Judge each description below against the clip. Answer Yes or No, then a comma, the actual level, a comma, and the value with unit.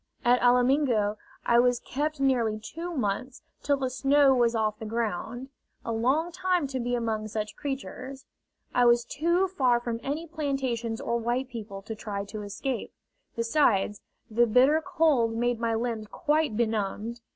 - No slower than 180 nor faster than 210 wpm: No, average, 160 wpm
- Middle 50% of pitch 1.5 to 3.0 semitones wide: No, average, 3.5 semitones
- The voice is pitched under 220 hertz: No, high, 240 Hz